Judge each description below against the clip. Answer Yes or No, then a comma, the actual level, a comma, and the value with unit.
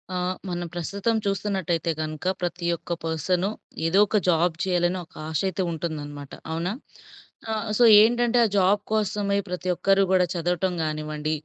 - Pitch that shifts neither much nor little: Yes, average, 3.2 semitones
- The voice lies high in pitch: No, medium, 180 Hz